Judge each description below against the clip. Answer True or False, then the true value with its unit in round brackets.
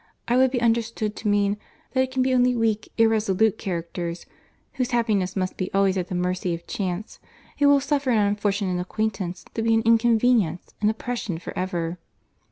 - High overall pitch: True (215 Hz)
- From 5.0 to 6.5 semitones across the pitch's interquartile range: False (4.2 semitones)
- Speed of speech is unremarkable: True (180 wpm)